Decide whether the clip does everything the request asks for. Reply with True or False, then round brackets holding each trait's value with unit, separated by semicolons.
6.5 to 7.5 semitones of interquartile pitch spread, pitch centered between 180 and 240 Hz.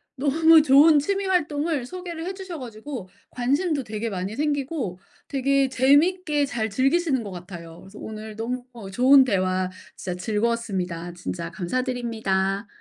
False (6.9 semitones; 250 Hz)